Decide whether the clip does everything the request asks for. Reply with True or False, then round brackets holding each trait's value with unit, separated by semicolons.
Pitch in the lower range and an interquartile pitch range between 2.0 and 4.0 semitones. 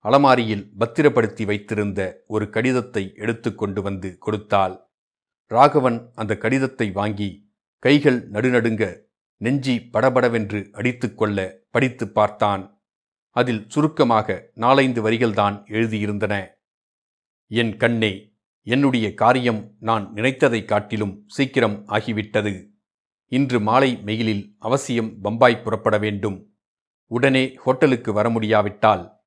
True (110 Hz; 2.9 semitones)